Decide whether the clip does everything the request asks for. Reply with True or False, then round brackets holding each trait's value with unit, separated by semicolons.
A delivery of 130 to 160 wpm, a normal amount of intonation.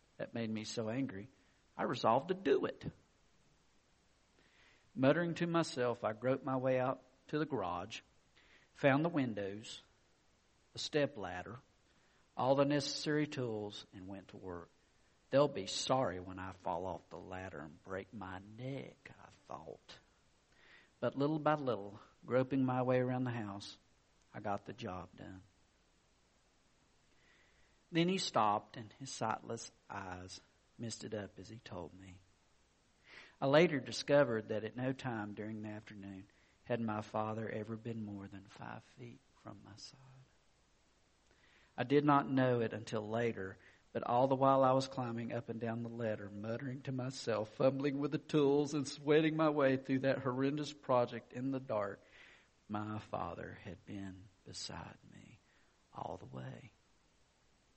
True (150 wpm; 5.0 semitones)